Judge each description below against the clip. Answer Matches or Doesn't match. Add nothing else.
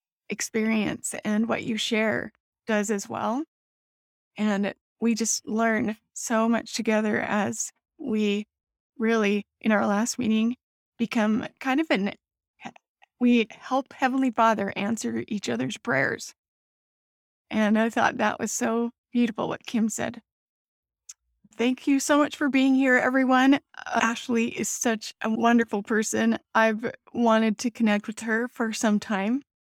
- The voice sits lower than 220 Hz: Doesn't match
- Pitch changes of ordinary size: Doesn't match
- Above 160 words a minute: Doesn't match